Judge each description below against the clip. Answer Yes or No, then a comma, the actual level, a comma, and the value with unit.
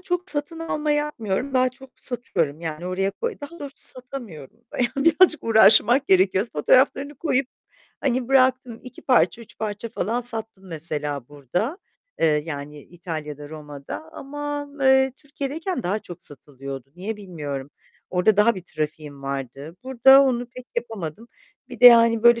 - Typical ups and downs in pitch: No, wide, 8.8 semitones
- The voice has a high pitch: Yes, high, 230 Hz